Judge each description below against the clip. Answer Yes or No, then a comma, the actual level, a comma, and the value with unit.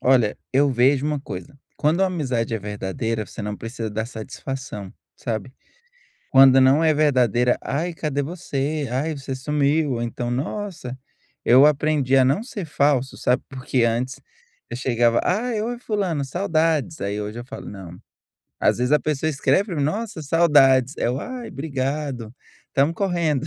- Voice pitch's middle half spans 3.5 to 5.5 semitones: Yes, average, 4.3 semitones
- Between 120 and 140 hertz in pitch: Yes, low, 135 Hz